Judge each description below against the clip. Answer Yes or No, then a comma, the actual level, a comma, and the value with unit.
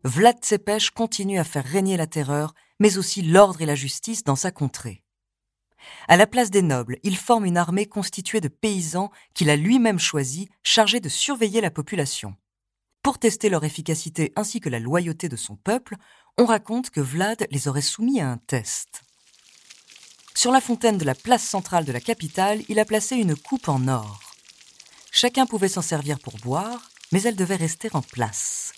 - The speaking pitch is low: No, medium, 185 Hz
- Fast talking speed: No, average, 185 wpm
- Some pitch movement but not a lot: No, wide, 7.2 semitones